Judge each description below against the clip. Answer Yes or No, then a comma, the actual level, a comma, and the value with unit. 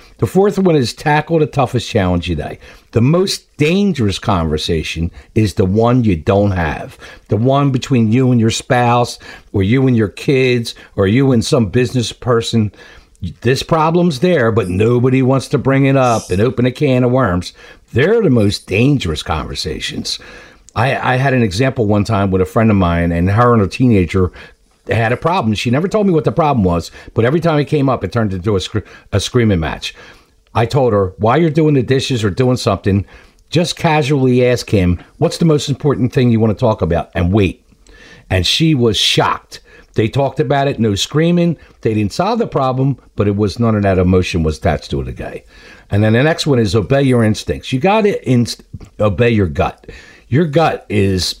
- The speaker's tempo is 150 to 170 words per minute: No, fast, 205 wpm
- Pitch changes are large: Yes, wide, 5.7 semitones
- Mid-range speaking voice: No, low, 115 Hz